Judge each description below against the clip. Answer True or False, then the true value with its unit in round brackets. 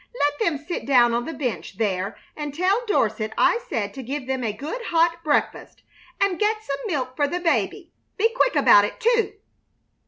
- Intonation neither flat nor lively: False (7.3 semitones)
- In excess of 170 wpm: True (190 wpm)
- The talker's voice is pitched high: True (290 Hz)